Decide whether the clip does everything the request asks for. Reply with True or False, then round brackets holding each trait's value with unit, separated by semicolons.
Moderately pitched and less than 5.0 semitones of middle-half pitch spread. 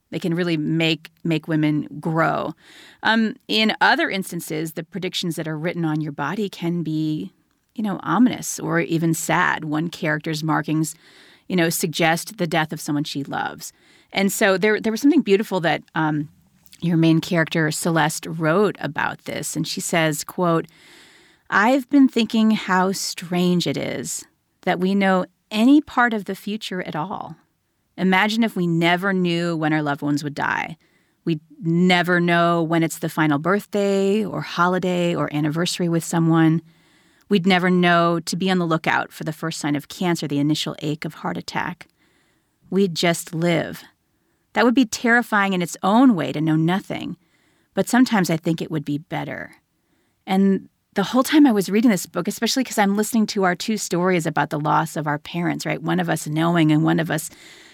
True (175 Hz; 3.6 semitones)